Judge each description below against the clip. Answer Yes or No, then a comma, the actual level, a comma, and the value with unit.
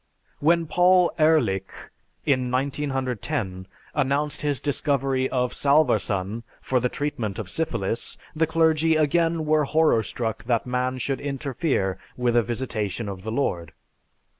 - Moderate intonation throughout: Yes, average, 4.8 semitones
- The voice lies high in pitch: No, low, 135 Hz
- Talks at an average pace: No, slow, 130 wpm